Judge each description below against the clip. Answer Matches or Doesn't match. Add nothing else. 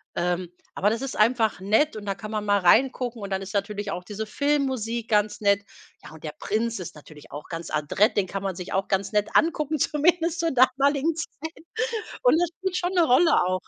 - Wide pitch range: Matches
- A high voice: Matches